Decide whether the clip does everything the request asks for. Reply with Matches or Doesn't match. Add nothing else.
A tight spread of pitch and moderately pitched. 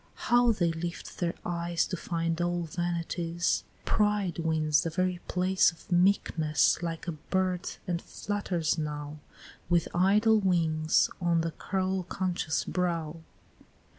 Matches